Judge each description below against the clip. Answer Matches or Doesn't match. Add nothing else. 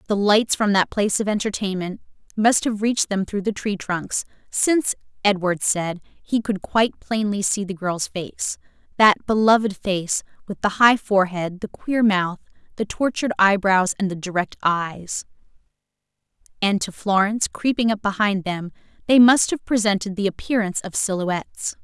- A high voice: Matches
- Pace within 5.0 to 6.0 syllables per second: Doesn't match